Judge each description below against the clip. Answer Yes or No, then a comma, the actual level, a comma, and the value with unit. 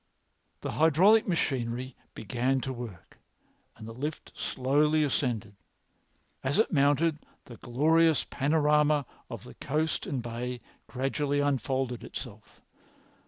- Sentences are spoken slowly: Yes, slow, 120 wpm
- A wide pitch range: No, average, 3.5 semitones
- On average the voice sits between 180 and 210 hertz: No, low, 135 Hz